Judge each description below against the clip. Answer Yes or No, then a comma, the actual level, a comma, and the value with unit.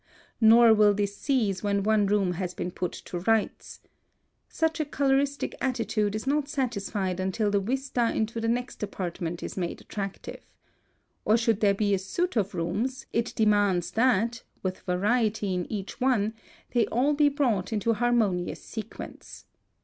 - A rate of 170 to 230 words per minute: No, average, 160 wpm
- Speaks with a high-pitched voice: Yes, high, 215 Hz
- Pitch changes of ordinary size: Yes, average, 3.7 semitones